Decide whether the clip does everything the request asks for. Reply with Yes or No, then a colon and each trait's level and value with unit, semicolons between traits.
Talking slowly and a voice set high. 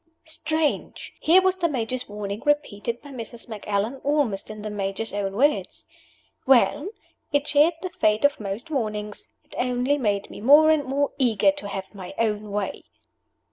No: average, 165 wpm; high, 240 Hz